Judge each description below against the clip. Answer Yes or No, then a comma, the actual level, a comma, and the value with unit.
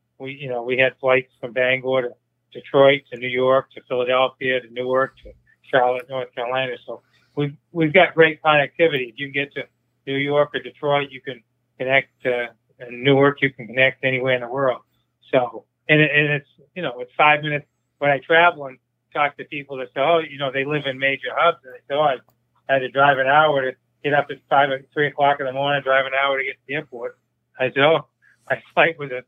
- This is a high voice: No, low, 135 Hz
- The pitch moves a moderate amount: No, narrow, 2.2 semitones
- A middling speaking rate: No, fast, 225 wpm